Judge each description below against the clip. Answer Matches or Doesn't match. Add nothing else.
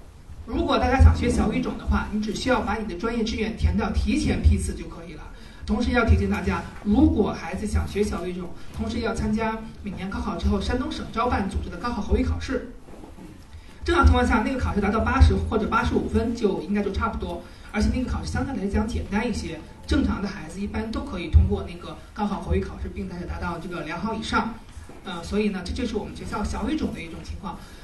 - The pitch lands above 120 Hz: Matches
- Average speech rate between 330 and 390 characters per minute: Matches